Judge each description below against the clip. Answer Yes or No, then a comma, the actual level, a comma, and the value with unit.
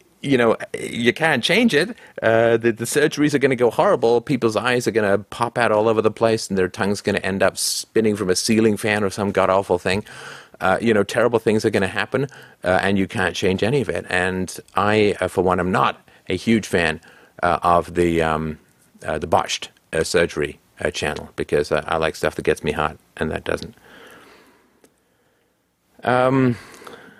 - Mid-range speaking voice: No, low, 105 Hz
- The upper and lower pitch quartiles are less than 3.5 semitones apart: No, average, 3.8 semitones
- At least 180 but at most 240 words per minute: Yes, fast, 205 wpm